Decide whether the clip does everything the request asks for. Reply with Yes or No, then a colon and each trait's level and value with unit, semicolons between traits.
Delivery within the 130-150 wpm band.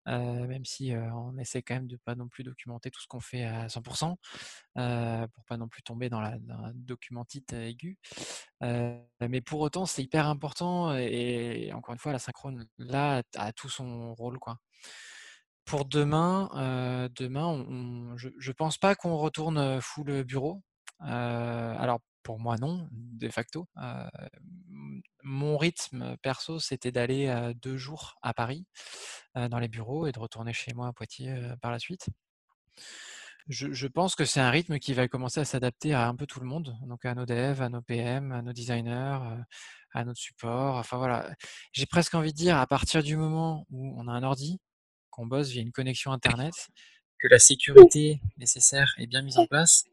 No: average, 195 wpm